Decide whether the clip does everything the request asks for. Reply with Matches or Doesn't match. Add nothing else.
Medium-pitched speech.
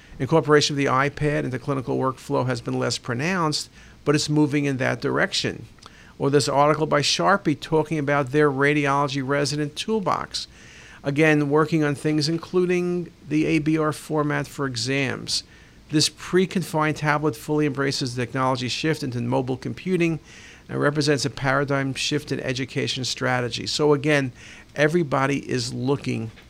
Matches